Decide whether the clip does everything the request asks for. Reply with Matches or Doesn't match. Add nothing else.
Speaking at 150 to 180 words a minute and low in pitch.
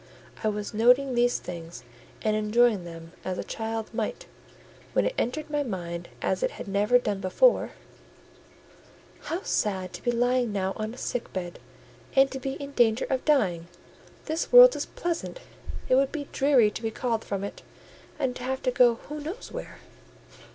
Doesn't match